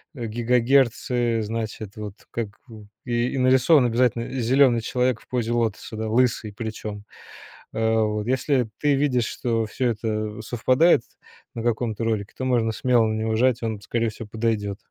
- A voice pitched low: Yes, low, 115 Hz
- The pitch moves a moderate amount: No, narrow, 2.3 semitones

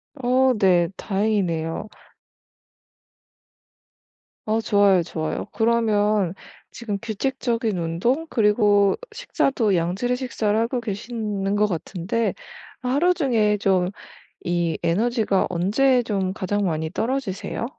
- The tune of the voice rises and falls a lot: No, average, 4.0 semitones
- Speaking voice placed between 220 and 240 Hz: No, high, 210 Hz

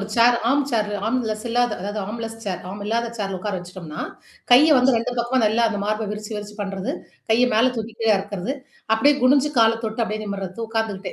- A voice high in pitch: Yes, high, 220 Hz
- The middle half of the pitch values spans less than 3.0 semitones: Yes, narrow, 2.6 semitones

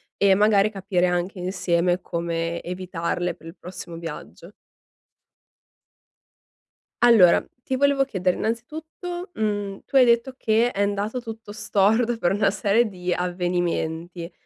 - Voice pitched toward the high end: Yes, high, 195 Hz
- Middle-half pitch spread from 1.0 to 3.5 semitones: No, average, 4.1 semitones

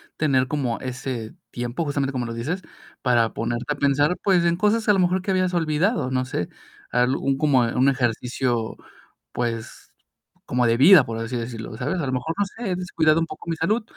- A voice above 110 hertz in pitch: Yes, low, 135 Hz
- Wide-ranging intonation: Yes, wide, 5.9 semitones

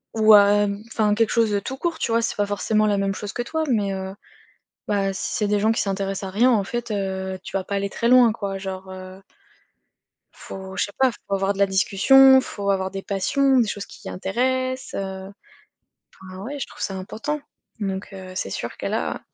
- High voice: Yes, high, 200 Hz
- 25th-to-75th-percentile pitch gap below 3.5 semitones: Yes, average, 3.0 semitones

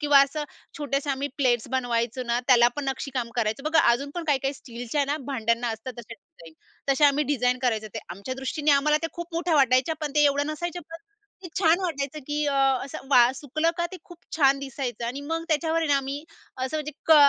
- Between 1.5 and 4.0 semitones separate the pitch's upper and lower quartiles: Yes, average, 3.4 semitones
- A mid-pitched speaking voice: No, very high, 280 Hz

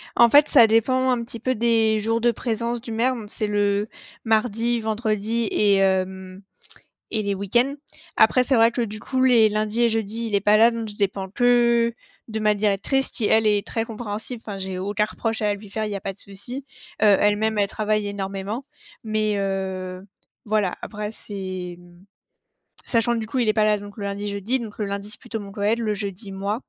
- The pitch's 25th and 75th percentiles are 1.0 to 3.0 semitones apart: Yes, narrow, 2.4 semitones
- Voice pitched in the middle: No, high, 215 Hz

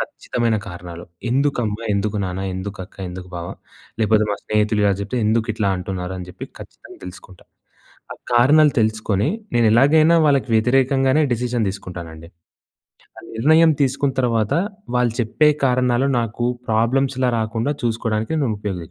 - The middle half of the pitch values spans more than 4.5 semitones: No, average, 4.2 semitones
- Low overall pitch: Yes, low, 115 Hz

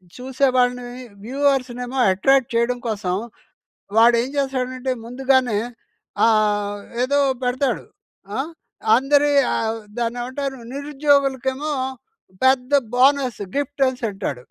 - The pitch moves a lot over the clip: No, narrow, 2.4 semitones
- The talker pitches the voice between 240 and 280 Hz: Yes, very high, 255 Hz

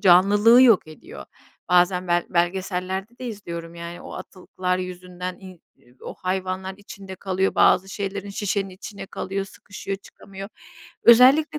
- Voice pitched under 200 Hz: Yes, high, 190 Hz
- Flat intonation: Yes, narrow, 1.8 semitones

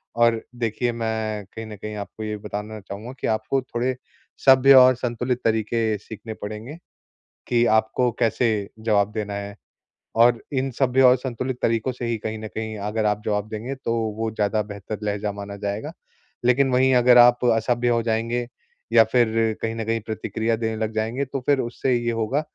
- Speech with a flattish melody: Yes, narrow, 2.2 semitones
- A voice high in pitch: No, low, 115 Hz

